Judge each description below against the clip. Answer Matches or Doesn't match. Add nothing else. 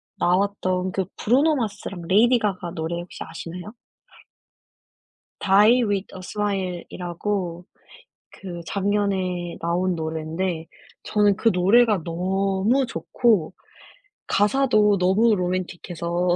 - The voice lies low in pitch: Doesn't match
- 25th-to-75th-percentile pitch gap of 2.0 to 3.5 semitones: Matches